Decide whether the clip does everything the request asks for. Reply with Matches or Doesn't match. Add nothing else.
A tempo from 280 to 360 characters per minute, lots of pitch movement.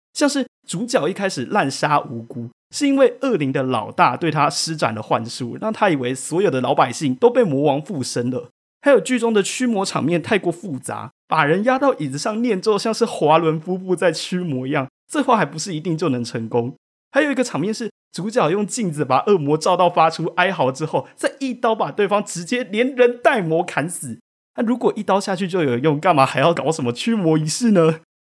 Matches